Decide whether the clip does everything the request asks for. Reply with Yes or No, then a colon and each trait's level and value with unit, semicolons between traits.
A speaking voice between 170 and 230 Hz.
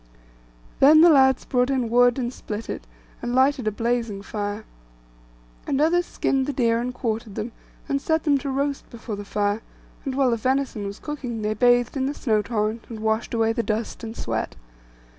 No: high, 240 Hz